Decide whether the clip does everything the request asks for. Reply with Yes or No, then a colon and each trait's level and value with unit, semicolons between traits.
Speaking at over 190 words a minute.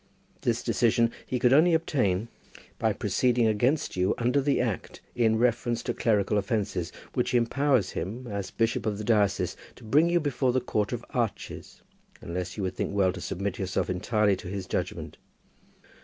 No: average, 170 wpm